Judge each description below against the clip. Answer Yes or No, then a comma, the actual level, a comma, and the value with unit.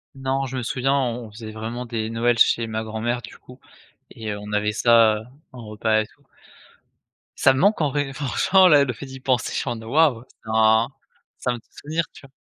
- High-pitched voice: No, low, 120 Hz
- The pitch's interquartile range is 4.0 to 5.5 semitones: No, average, 3.3 semitones